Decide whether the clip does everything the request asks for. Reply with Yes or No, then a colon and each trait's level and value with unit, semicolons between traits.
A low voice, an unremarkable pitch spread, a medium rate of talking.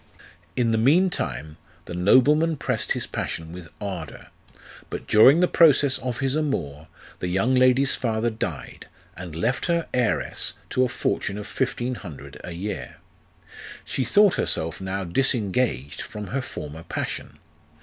No: low, 115 Hz; wide, 6.8 semitones; average, 150 wpm